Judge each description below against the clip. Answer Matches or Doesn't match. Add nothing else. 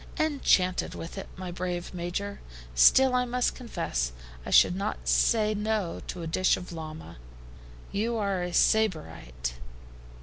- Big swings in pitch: Doesn't match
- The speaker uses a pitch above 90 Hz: Matches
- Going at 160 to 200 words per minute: Doesn't match